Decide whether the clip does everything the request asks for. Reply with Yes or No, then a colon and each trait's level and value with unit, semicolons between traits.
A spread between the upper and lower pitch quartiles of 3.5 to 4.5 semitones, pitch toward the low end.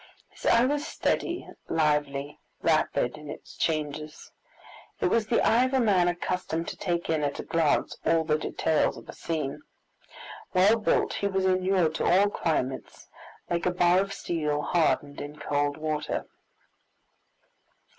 No: average, 4.0 semitones; medium, 165 Hz